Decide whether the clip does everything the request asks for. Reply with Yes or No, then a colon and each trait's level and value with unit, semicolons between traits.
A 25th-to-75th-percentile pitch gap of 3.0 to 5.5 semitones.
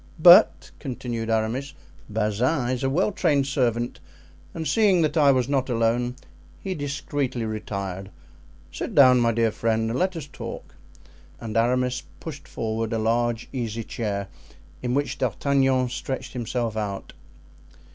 Yes: average, 3.5 semitones